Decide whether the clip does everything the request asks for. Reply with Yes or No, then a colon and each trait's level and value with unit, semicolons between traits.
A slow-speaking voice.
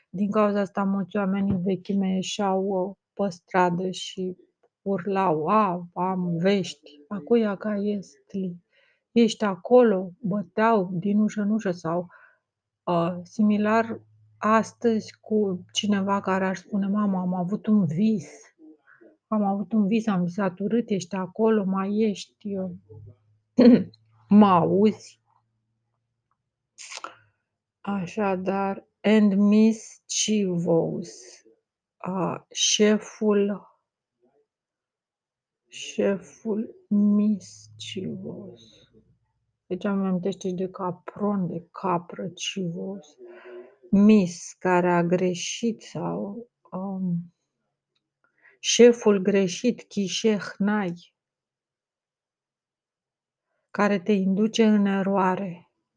Yes: slow, 90 wpm